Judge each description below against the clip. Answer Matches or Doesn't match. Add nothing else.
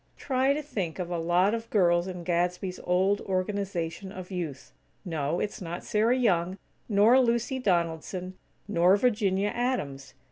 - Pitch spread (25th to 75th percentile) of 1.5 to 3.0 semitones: Doesn't match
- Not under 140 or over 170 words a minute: Matches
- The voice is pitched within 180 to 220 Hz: Matches